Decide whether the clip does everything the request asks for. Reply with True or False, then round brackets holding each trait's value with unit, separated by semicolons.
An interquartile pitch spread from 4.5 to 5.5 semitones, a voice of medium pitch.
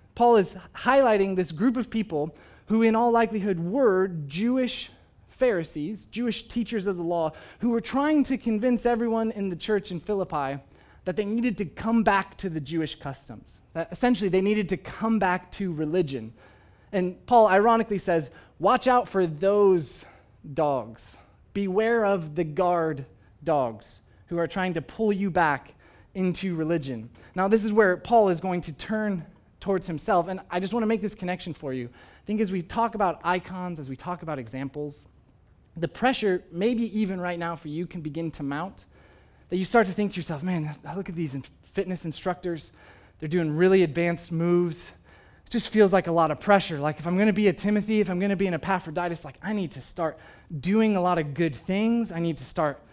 True (4.9 semitones; 180 Hz)